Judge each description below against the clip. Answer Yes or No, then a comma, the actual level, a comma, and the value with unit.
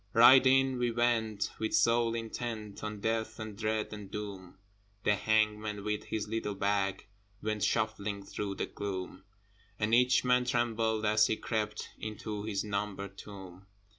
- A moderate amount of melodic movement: No, narrow, 1.8 semitones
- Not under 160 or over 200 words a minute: No, average, 150 wpm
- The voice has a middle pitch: No, low, 110 Hz